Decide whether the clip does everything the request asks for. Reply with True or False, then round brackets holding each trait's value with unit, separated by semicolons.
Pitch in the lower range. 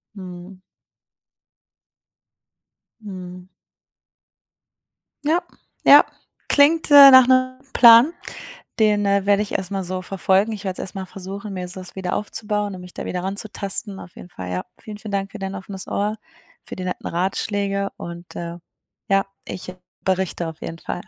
False (195 Hz)